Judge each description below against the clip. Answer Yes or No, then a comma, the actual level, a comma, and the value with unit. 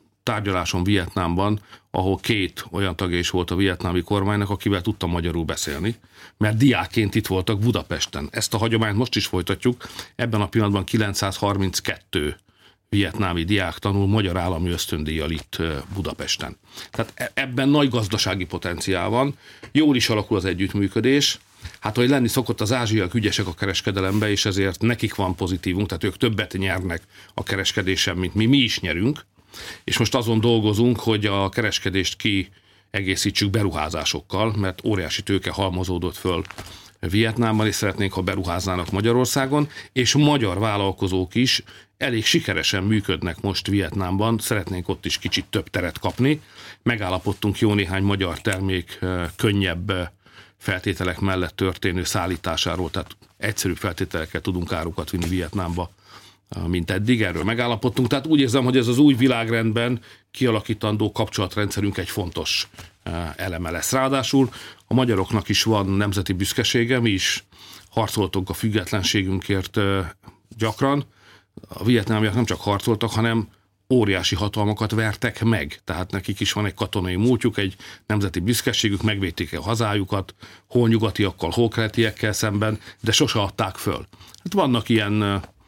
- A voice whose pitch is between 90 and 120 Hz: Yes, low, 100 Hz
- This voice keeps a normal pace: Yes, average, 135 wpm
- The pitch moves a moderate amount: Yes, average, 3.2 semitones